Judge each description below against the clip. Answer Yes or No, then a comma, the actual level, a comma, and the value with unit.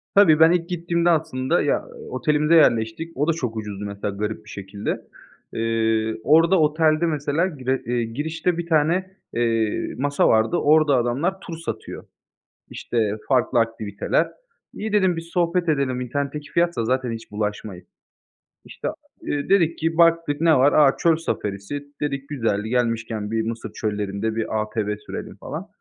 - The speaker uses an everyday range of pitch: No, wide, 6.6 semitones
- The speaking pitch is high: No, medium, 140 Hz